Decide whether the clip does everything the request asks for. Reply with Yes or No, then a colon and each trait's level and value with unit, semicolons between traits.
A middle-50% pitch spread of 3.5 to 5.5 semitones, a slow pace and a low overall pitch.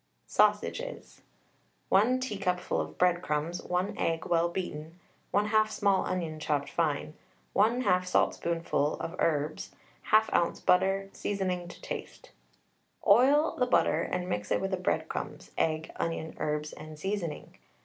No: average, 4.0 semitones; slow, 130 wpm; medium, 180 Hz